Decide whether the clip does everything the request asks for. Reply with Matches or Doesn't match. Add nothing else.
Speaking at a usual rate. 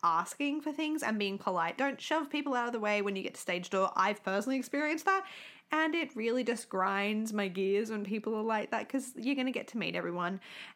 Doesn't match